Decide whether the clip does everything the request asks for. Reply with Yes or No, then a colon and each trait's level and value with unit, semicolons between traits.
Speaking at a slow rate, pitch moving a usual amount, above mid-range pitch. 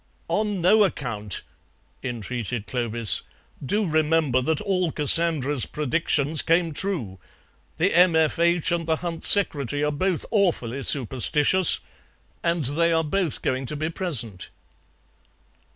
No: slow, 120 wpm; average, 4.8 semitones; medium, 155 Hz